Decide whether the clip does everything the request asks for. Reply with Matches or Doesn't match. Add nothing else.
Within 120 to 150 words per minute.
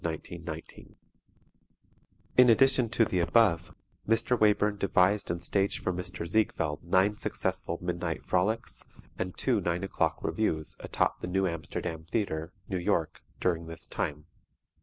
Matches